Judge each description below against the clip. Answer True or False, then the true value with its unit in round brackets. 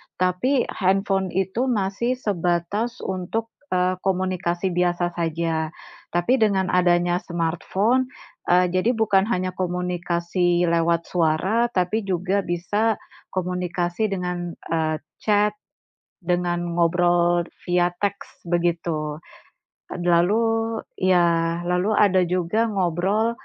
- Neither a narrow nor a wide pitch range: False (2.3 semitones)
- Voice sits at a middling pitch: True (180 Hz)